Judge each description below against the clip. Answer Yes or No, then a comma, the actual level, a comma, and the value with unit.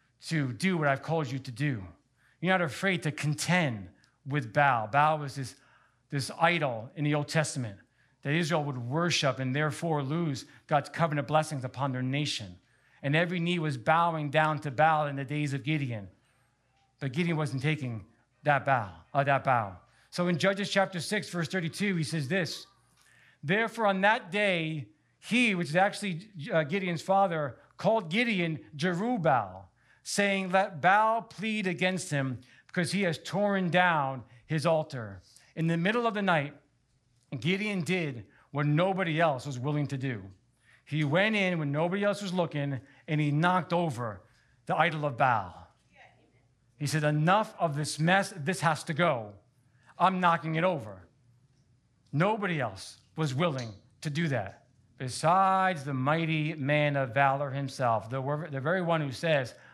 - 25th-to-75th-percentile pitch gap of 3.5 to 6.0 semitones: Yes, average, 4.8 semitones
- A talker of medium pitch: Yes, medium, 150 Hz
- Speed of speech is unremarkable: Yes, average, 160 wpm